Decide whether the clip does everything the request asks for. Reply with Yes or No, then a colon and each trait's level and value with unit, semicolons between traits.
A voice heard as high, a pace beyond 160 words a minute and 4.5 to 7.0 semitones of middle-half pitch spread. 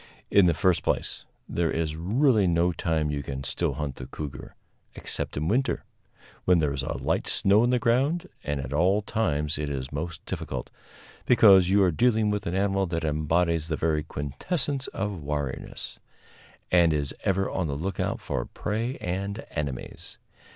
No: very low, 85 Hz; average, 170 wpm; average, 5.2 semitones